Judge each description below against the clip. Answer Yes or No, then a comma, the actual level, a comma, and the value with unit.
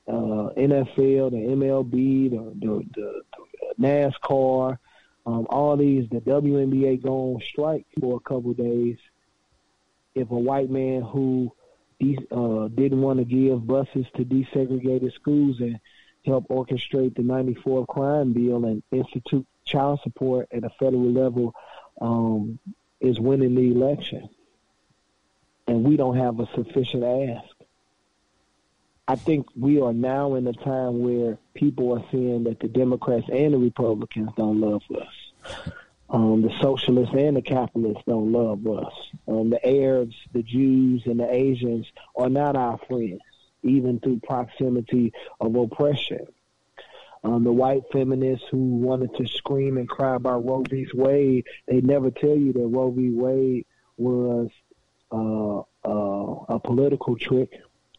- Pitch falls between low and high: No, low, 125 Hz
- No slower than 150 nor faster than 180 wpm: No, average, 140 wpm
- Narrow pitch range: Yes, narrow, 2.1 semitones